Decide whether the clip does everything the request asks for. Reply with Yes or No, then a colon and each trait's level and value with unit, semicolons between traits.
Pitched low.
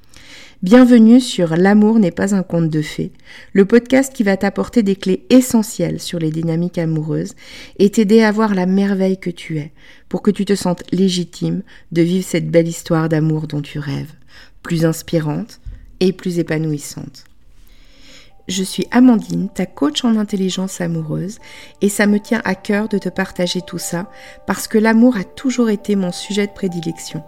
No: medium, 185 Hz